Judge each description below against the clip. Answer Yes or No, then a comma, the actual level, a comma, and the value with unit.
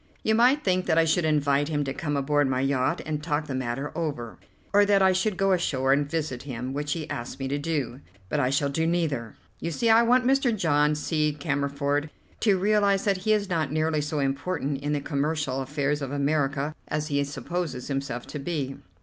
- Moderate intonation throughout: Yes, average, 3.8 semitones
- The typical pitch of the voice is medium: Yes, medium, 150 Hz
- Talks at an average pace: No, fast, 210 wpm